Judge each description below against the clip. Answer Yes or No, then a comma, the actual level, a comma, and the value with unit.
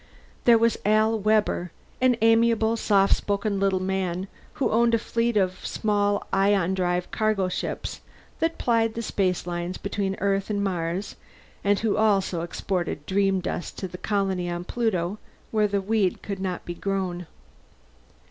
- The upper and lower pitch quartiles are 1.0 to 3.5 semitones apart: Yes, average, 2.8 semitones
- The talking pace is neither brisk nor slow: Yes, average, 150 wpm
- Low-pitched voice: No, high, 200 Hz